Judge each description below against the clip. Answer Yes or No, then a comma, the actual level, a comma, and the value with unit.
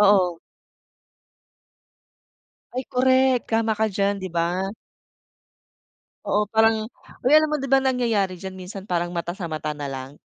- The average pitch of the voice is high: Yes, high, 200 Hz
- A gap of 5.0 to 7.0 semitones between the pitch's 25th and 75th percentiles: Yes, wide, 5.6 semitones